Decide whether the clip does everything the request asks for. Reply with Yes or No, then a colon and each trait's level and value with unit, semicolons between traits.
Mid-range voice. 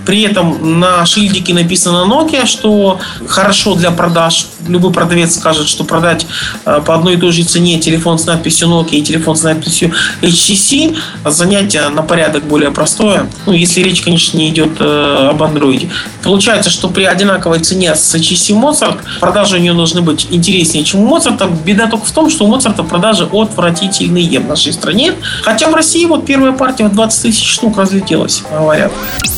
Yes: medium, 175 Hz